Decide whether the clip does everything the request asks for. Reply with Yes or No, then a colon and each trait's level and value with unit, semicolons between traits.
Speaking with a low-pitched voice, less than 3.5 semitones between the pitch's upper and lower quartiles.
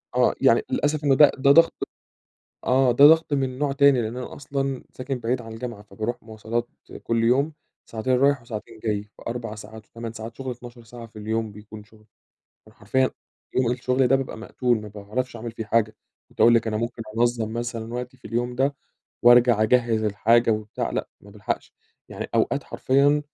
Yes: low, 120 Hz; average, 2.8 semitones